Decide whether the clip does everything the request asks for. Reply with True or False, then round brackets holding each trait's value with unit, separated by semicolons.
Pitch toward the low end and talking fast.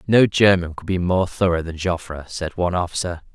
False (90 Hz; 195 wpm)